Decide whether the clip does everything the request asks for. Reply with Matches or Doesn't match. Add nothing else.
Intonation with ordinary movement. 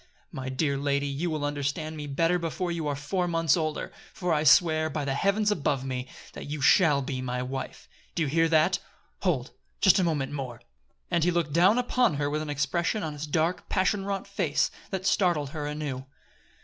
Matches